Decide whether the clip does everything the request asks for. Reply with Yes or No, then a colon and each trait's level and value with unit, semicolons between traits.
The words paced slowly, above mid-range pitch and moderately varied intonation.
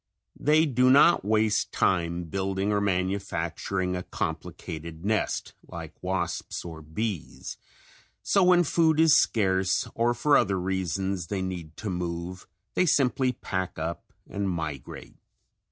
No: slow, 130 wpm; very low, 95 Hz; average, 4.7 semitones